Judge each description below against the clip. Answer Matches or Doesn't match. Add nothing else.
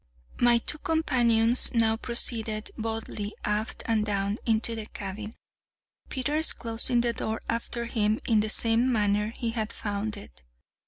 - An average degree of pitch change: Doesn't match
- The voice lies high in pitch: Matches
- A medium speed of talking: Matches